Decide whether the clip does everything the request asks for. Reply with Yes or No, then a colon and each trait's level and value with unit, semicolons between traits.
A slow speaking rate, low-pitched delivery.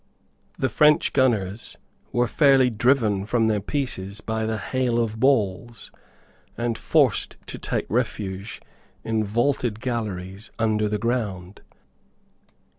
Yes: slow, 115 wpm; low, 110 Hz